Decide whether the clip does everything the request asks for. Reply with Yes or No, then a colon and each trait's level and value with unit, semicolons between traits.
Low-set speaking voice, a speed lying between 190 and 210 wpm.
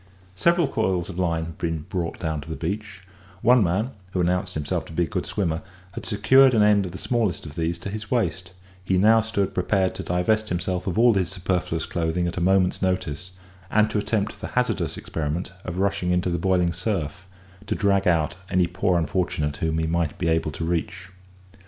Yes: very low, 90 Hz; fast, 205 wpm